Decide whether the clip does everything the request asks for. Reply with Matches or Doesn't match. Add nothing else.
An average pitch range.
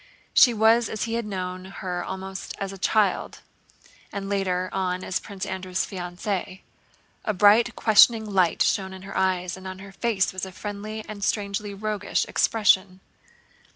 Doesn't match